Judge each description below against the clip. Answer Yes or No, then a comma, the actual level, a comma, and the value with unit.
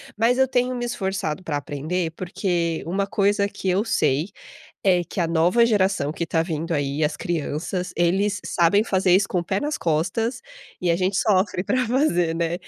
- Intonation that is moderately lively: Yes, average, 3.6 semitones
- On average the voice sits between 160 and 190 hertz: Yes, medium, 185 Hz